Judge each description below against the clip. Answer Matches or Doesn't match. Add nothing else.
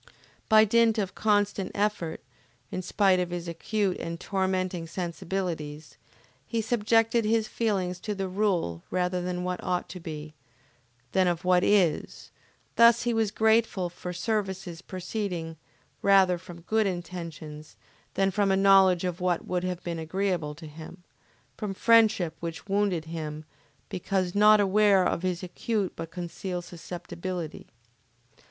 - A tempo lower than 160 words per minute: Matches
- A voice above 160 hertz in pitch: Matches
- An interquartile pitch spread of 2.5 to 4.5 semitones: Matches